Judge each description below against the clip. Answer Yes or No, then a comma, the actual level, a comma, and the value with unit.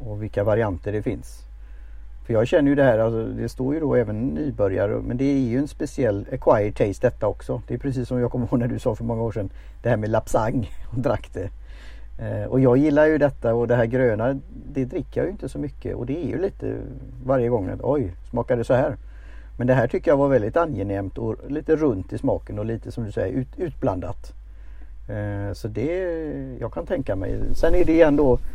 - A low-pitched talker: Yes, low, 120 Hz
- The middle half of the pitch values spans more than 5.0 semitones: No, average, 4.2 semitones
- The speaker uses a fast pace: Yes, fast, 230 wpm